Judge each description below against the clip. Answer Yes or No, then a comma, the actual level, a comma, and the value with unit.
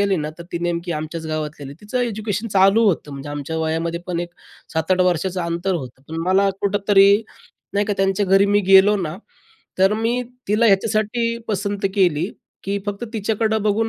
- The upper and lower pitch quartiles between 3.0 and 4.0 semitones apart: Yes, average, 3.5 semitones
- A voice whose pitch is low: No, high, 195 Hz